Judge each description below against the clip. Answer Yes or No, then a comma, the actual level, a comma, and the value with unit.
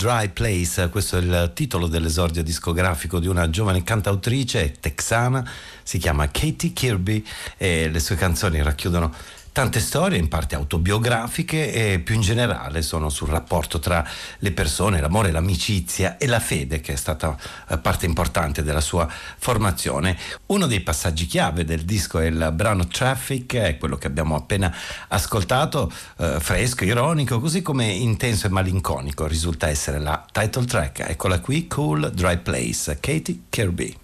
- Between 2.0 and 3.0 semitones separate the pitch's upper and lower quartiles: No, average, 5.2 semitones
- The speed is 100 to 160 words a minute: Yes, average, 150 wpm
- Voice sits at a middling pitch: No, very low, 90 Hz